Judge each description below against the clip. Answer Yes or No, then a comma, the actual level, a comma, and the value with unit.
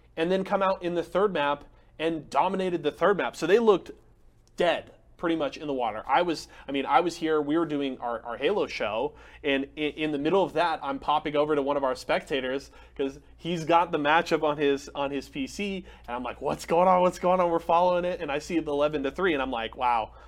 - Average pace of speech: No, fast, 250 wpm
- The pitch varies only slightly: No, average, 3.6 semitones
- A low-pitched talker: No, medium, 155 Hz